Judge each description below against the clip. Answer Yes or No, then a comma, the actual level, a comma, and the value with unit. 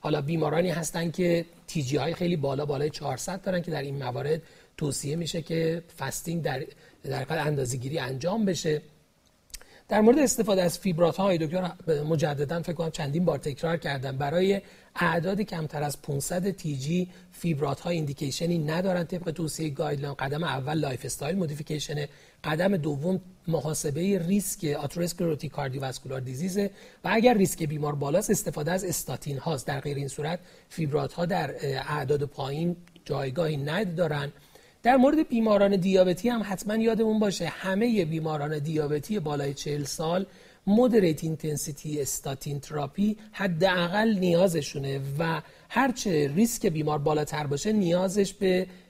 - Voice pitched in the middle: Yes, medium, 165 Hz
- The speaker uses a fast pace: No, average, 140 wpm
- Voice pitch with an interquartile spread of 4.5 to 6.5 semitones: No, average, 3.8 semitones